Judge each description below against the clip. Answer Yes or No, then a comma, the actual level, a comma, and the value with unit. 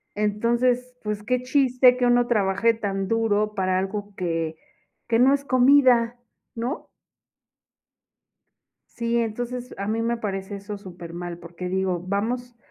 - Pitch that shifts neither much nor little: Yes, average, 4.0 semitones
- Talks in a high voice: Yes, high, 220 Hz